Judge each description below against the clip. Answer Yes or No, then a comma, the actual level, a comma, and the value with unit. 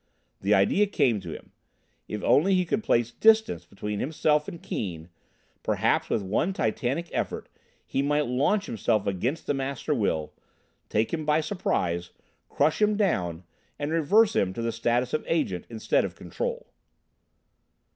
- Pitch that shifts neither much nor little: No, wide, 8.3 semitones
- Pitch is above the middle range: No, low, 135 Hz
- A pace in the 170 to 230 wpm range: No, average, 155 wpm